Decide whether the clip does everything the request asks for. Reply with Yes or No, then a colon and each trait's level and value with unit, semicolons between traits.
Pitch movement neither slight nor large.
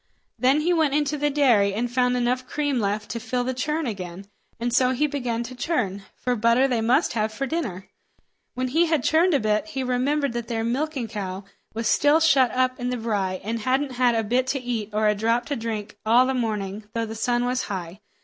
Yes: average, 3.5 semitones